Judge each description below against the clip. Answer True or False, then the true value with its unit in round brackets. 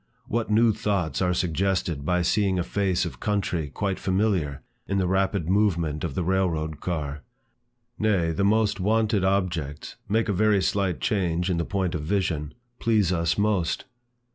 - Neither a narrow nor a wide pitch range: True (3.4 semitones)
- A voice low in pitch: True (95 Hz)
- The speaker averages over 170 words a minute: False (165 wpm)